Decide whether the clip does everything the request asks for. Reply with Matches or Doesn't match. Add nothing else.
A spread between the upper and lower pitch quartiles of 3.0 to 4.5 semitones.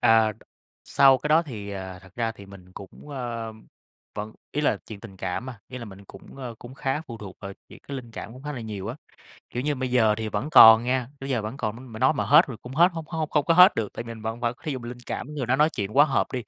Matches